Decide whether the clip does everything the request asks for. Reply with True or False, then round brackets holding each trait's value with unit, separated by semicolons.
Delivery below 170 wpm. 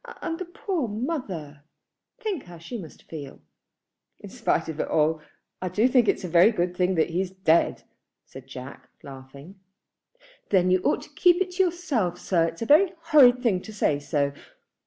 False (180 wpm)